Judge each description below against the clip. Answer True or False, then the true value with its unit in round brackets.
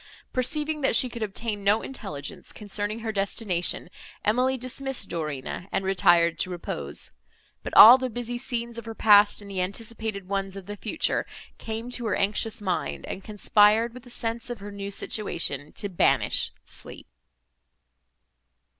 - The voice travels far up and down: False (3.4 semitones)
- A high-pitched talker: True (210 Hz)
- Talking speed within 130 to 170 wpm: True (155 wpm)